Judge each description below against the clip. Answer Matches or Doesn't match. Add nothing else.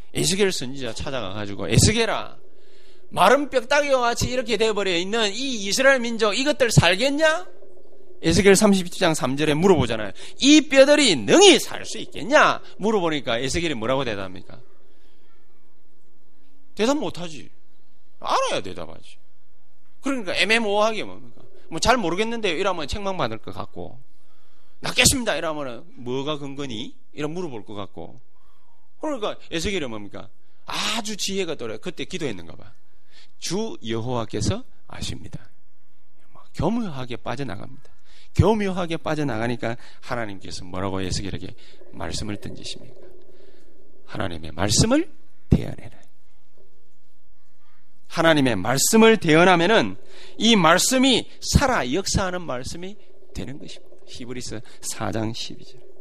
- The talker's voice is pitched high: Doesn't match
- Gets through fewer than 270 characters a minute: Doesn't match